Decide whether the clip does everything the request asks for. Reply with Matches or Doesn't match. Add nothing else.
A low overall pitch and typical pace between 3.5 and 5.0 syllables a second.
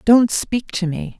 Doesn't match